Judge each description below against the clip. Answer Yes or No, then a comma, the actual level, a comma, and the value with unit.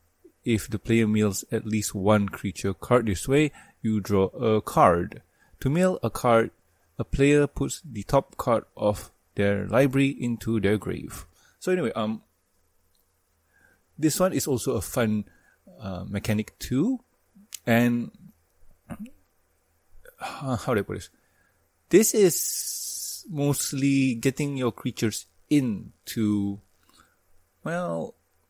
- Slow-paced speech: Yes, slow, 125 wpm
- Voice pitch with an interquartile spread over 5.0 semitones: Yes, wide, 5.5 semitones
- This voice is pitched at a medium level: No, low, 115 Hz